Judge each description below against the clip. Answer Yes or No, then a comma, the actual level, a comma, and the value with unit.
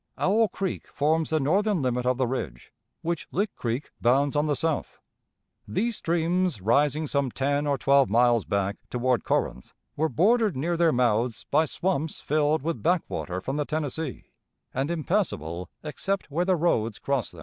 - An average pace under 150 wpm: No, average, 165 wpm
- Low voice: No, medium, 145 Hz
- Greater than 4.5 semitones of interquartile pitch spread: Yes, average, 5.2 semitones